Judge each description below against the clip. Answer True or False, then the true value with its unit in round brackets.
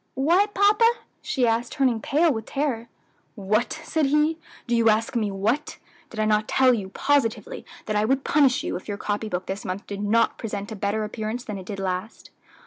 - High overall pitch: True (230 Hz)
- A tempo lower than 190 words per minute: False (205 wpm)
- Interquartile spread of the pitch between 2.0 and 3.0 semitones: False (4.9 semitones)